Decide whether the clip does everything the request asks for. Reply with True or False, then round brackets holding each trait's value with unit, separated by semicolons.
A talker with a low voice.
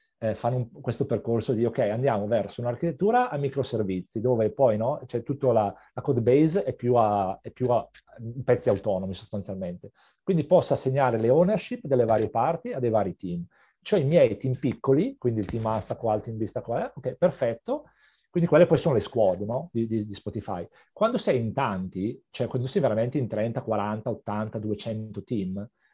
True (120 Hz)